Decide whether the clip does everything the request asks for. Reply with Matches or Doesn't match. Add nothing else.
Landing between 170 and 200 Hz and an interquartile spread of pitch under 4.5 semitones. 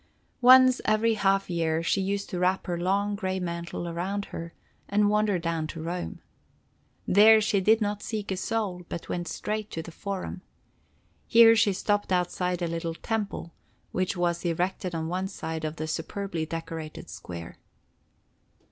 Matches